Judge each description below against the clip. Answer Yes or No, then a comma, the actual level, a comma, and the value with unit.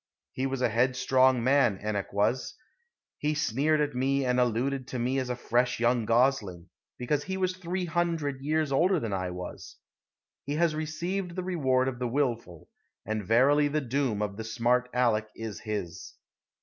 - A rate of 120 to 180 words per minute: Yes, average, 175 wpm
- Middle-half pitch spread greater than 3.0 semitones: Yes, average, 4.2 semitones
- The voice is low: Yes, low, 130 Hz